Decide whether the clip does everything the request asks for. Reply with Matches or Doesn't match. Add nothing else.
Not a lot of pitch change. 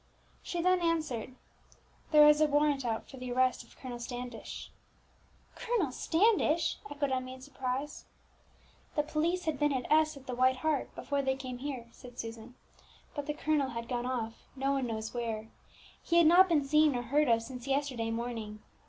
Doesn't match